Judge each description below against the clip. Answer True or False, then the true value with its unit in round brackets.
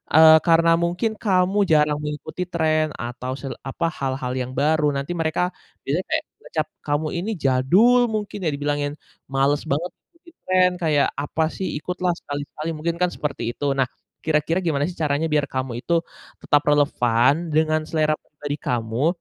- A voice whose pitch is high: False (155 Hz)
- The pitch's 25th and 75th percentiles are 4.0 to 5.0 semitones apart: False (3.3 semitones)